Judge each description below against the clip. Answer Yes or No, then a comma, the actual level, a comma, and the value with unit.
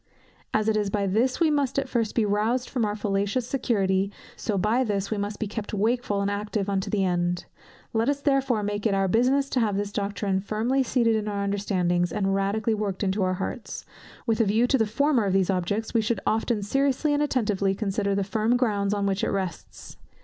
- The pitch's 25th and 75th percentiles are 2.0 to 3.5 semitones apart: Yes, average, 2.9 semitones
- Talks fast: Yes, fast, 215 wpm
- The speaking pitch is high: Yes, high, 210 Hz